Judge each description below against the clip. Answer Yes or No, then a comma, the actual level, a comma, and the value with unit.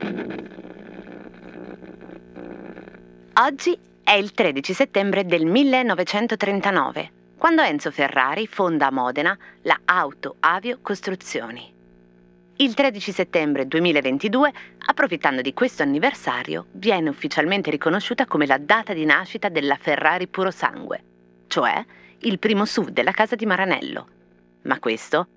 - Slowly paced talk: Yes, slow, 110 wpm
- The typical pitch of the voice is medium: Yes, medium, 165 Hz